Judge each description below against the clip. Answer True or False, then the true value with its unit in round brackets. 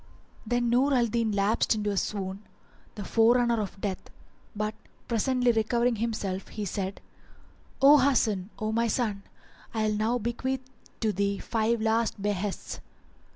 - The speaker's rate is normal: True (145 wpm)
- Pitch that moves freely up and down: False (2.6 semitones)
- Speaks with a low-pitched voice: False (220 Hz)